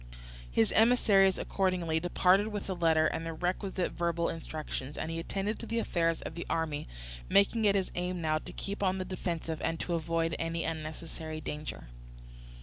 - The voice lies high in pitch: No, medium, 170 Hz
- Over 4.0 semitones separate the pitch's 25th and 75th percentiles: No, average, 3.0 semitones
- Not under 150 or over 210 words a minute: Yes, average, 175 wpm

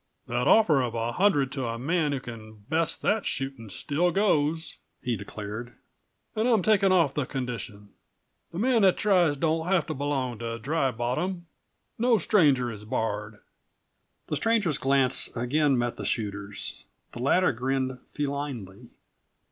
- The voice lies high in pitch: No, low, 135 Hz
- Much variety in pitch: Yes, wide, 6.0 semitones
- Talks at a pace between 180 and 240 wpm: No, average, 150 wpm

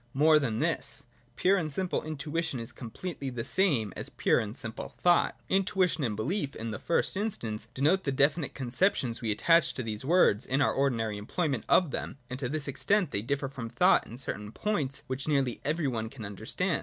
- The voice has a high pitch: No, medium, 140 Hz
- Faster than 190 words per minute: Yes, average, 200 wpm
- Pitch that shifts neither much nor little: No, wide, 6.4 semitones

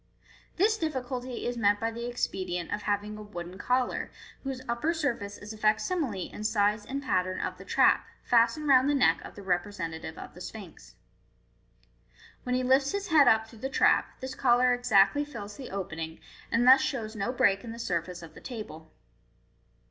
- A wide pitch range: No, average, 4.5 semitones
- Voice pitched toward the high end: Yes, high, 225 Hz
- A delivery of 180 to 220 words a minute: Yes, average, 185 wpm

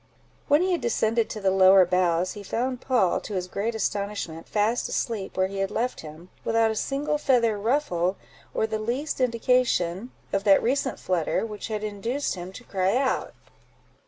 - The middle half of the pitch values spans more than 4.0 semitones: Yes, average, 4.5 semitones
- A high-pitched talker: Yes, high, 215 Hz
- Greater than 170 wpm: Yes, average, 180 wpm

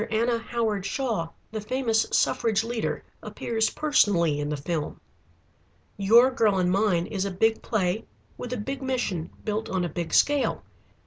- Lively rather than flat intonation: No, average, 4.5 semitones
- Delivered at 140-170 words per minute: Yes, average, 155 wpm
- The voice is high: Yes, high, 215 Hz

